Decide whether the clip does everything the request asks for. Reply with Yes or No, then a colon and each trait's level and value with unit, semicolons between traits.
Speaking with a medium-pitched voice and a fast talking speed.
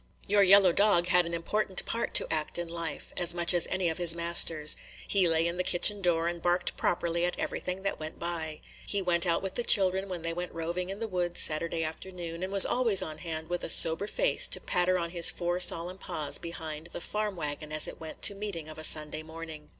Yes: medium, 175 Hz; fast, 230 wpm